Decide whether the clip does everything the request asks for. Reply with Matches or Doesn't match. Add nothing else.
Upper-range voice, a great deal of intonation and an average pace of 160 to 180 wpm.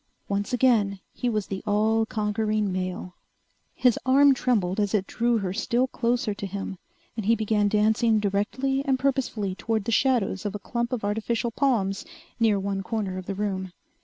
Doesn't match